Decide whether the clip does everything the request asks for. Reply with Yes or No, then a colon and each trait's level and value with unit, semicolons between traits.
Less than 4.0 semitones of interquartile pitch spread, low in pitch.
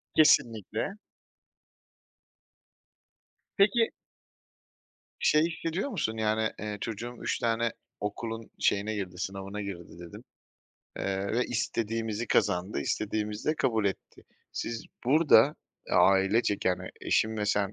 Yes: average, 2.9 semitones; low, 110 Hz